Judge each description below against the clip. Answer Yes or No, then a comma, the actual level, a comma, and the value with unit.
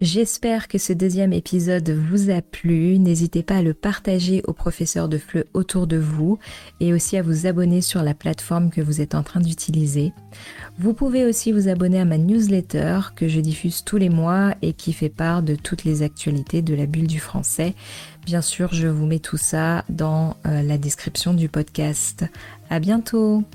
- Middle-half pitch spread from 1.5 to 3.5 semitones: Yes, average, 3.1 semitones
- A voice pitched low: No, medium, 170 Hz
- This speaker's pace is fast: No, average, 190 wpm